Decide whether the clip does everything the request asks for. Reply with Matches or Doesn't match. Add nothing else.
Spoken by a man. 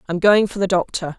Doesn't match